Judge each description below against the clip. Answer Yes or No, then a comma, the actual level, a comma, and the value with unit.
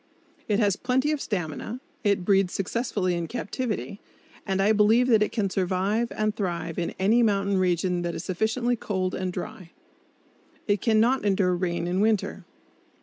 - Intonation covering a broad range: No, average, 3.3 semitones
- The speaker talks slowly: No, average, 165 wpm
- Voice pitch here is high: Yes, high, 200 Hz